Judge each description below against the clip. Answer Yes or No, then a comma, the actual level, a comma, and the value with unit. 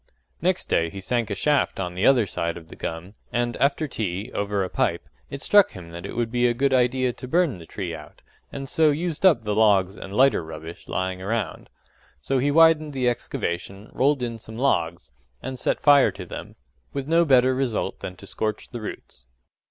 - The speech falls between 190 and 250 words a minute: Yes, fast, 205 wpm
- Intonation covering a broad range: Yes, wide, 6.4 semitones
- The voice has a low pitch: Yes, low, 120 Hz